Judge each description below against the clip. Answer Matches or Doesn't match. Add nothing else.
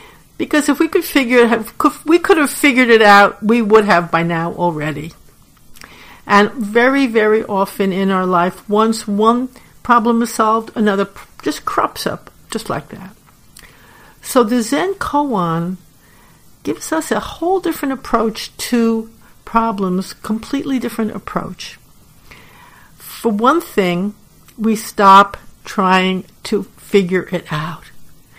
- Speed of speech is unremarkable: Doesn't match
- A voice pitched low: Doesn't match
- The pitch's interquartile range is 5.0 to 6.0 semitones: Doesn't match